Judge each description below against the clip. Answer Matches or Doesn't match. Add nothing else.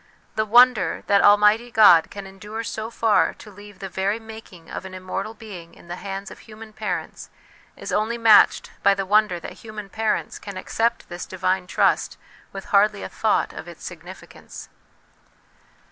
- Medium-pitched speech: Doesn't match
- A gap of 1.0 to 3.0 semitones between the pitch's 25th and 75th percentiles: Matches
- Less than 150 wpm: Doesn't match